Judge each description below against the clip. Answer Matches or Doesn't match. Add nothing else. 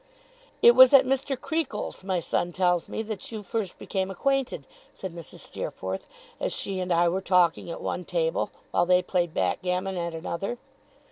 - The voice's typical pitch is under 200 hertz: Matches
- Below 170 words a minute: Doesn't match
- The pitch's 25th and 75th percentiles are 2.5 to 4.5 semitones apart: Doesn't match